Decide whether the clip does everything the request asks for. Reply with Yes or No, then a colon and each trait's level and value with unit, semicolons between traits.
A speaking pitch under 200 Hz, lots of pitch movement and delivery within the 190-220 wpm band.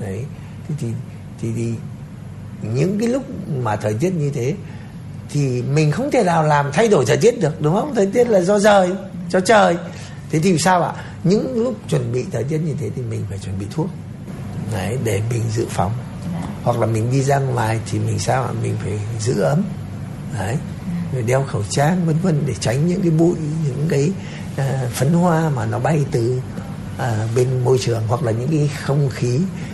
Yes: medium, 140 Hz; wide, 6.2 semitones; average, 200 wpm